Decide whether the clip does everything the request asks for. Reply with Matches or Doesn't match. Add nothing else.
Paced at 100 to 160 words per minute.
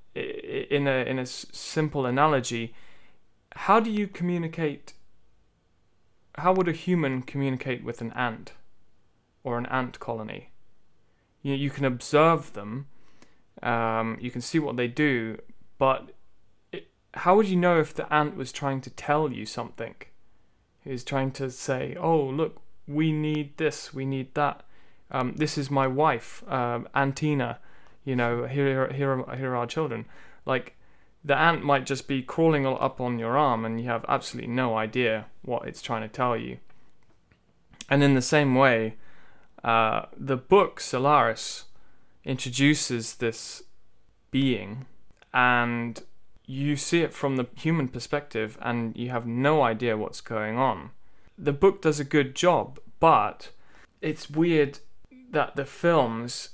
Matches